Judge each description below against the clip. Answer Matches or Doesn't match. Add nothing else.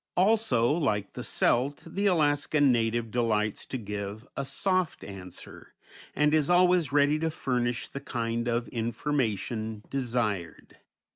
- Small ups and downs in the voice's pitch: Doesn't match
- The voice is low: Matches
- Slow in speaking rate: Matches